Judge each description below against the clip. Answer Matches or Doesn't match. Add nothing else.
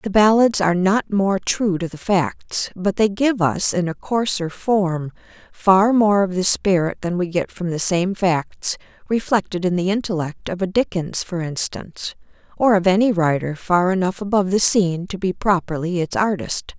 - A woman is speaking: Matches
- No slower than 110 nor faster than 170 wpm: Doesn't match